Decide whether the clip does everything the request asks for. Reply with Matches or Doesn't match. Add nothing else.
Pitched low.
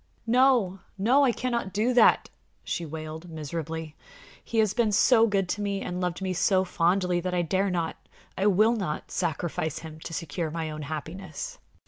Doesn't match